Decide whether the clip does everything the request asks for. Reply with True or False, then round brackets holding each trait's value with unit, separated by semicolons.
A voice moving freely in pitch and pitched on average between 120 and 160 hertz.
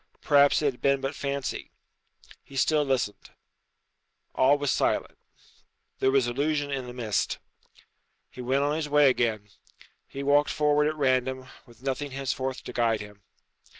False (2.4 semitones; 135 Hz)